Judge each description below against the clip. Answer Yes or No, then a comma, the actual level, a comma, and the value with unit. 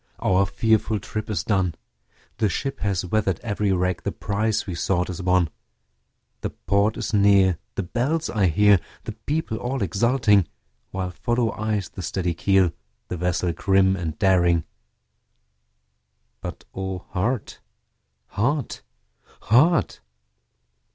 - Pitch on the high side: No, low, 100 Hz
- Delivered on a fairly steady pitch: No, average, 3.2 semitones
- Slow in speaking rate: Yes, slow, 130 wpm